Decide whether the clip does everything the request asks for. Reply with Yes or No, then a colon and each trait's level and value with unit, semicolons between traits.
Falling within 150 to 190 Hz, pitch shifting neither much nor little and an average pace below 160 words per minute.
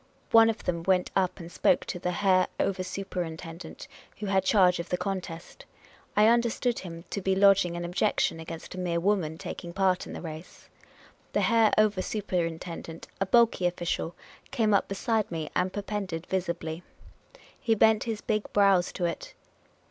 No: medium, 185 Hz; average, 3.2 semitones; average, 170 wpm